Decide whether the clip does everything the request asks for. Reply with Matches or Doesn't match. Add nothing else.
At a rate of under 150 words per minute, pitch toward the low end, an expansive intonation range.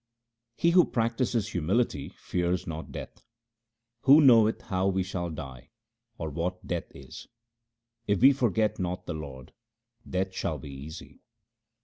Matches